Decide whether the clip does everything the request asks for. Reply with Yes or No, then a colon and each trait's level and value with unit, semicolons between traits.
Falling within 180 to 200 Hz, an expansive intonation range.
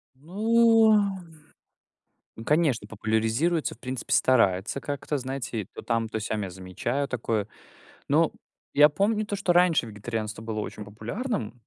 No: low, 130 Hz; wide, 8.1 semitones